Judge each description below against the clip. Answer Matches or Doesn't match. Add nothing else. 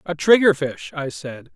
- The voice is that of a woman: Doesn't match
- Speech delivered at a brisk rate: Doesn't match